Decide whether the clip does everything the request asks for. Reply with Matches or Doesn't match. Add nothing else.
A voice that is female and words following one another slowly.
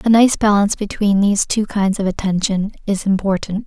Doesn't match